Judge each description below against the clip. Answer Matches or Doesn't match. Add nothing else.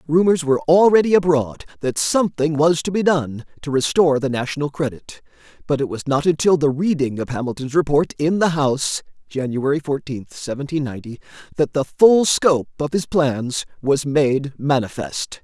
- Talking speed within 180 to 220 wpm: Doesn't match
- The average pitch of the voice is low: Doesn't match